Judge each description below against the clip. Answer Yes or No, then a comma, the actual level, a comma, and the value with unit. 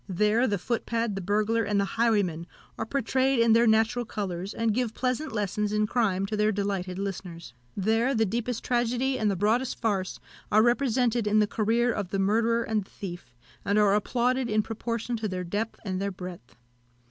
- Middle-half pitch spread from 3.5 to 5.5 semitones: No, average, 3.0 semitones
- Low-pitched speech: No, high, 215 Hz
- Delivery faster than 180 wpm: Yes, average, 190 wpm